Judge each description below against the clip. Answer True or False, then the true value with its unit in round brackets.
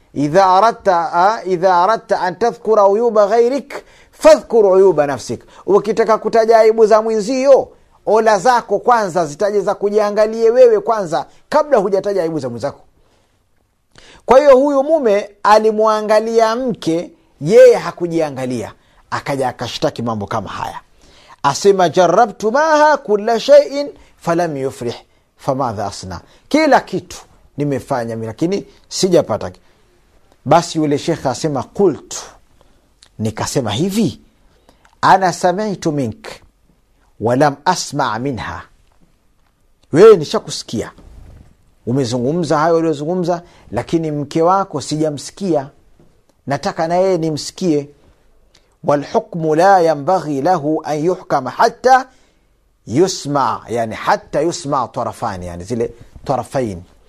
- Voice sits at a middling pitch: True (170 Hz)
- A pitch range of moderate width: False (8.2 semitones)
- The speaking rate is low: True (85 wpm)